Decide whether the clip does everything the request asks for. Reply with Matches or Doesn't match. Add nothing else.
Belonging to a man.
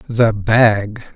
Matches